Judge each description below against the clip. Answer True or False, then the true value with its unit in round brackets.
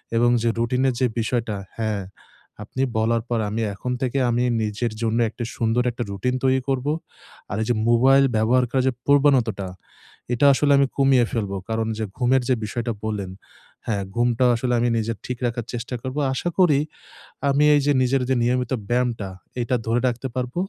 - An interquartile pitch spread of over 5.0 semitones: False (2.4 semitones)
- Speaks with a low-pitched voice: True (120 Hz)